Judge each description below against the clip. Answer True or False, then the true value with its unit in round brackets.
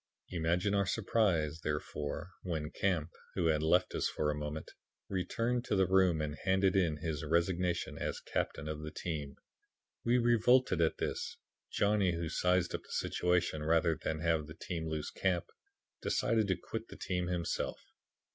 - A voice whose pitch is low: True (85 Hz)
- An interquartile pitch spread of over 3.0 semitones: True (3.4 semitones)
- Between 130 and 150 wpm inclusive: False (165 wpm)